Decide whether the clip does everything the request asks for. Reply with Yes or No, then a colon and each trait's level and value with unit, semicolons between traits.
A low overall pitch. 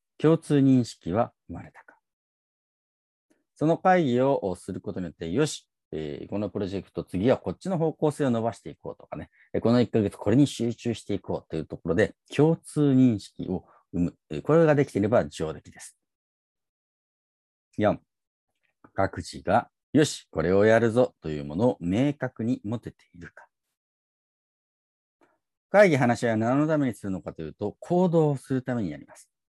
Yes: low, 120 Hz